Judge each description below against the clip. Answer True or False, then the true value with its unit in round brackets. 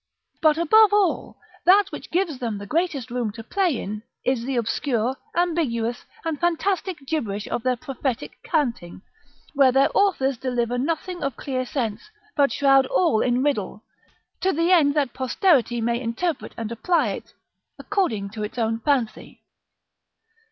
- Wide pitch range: True (6.0 semitones)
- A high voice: True (270 Hz)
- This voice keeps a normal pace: True (150 wpm)